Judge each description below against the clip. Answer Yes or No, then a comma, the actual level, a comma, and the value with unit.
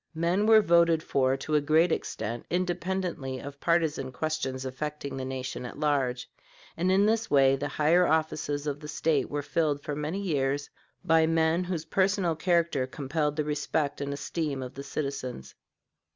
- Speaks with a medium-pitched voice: Yes, medium, 150 Hz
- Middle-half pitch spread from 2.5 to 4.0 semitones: Yes, average, 3.3 semitones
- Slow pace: No, average, 165 wpm